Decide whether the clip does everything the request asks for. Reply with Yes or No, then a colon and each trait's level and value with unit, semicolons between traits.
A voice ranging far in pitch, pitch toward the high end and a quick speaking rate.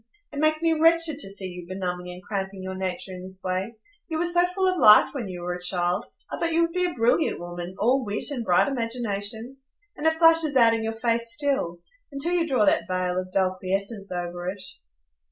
Yes: wide, 8.0 semitones; high, 215 Hz; fast, 220 wpm